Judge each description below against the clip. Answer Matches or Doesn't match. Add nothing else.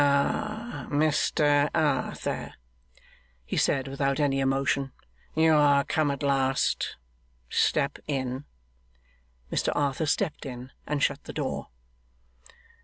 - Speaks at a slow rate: Matches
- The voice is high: Doesn't match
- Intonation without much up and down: Matches